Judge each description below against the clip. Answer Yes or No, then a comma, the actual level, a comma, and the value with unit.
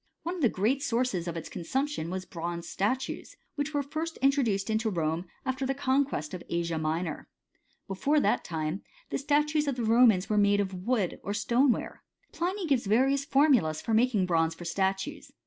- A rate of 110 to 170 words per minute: No, average, 180 wpm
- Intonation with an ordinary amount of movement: No, wide, 7.3 semitones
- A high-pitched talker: Yes, high, 220 Hz